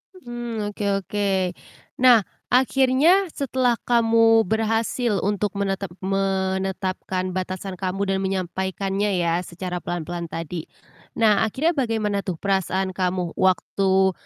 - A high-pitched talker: Yes, high, 195 Hz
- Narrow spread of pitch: No, average, 3.3 semitones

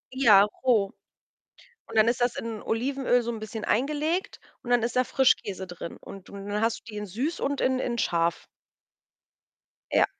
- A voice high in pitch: Yes, high, 230 Hz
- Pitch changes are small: No, average, 3.8 semitones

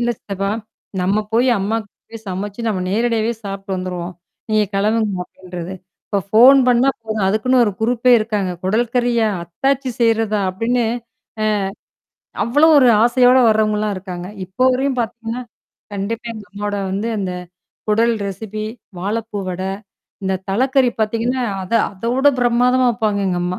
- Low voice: No, high, 220 Hz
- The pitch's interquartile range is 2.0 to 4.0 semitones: Yes, average, 3.5 semitones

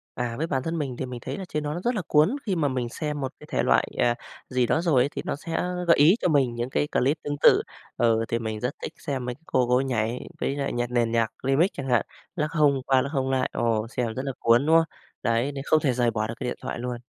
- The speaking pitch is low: Yes, low, 130 Hz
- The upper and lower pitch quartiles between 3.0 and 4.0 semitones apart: Yes, average, 3.6 semitones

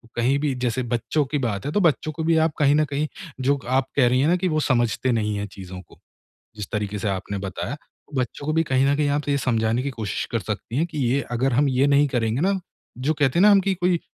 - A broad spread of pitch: No, average, 4.6 semitones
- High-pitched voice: No, low, 135 Hz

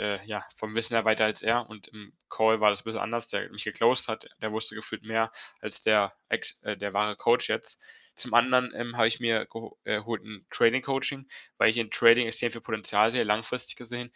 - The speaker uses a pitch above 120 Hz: No, low, 110 Hz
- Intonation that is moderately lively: No, narrow, 1.6 semitones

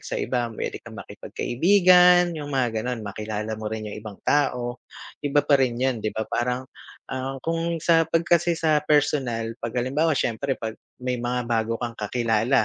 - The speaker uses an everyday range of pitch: Yes, average, 4.7 semitones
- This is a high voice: No, low, 125 Hz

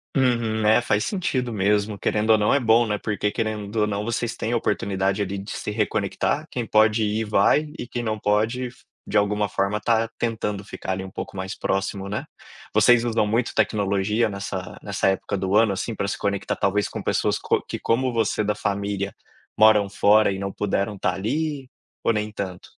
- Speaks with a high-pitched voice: No, low, 105 Hz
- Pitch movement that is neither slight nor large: No, narrow, 2.3 semitones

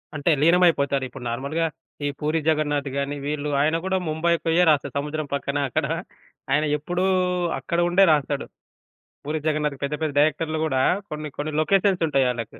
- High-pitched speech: No, medium, 150 Hz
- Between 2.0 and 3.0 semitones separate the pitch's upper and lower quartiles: Yes, narrow, 2.4 semitones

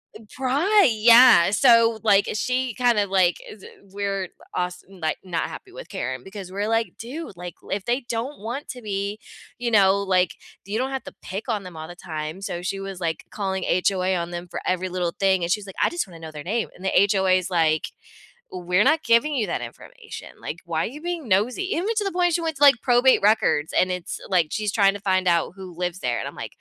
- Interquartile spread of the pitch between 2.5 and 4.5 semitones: No, average, 4.9 semitones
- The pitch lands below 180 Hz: No, high, 200 Hz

